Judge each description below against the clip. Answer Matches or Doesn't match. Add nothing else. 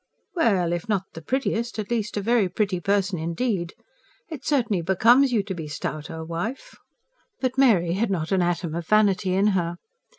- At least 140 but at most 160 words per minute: Doesn't match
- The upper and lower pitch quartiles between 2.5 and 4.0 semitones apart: Doesn't match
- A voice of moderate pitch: Doesn't match